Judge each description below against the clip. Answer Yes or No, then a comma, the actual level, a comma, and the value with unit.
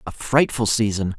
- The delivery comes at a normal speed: Yes, average, 150 wpm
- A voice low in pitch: Yes, low, 115 Hz